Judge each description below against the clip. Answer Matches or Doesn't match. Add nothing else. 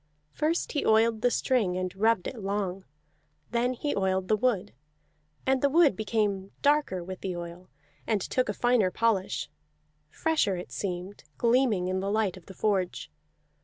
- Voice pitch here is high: Matches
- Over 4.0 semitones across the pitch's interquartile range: Matches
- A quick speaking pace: Doesn't match